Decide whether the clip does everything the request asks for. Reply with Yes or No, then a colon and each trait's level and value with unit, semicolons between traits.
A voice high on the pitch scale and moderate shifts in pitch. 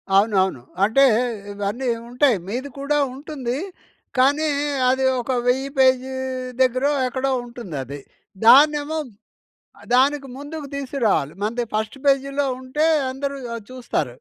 Yes: very high, 260 Hz; average, 3.2 semitones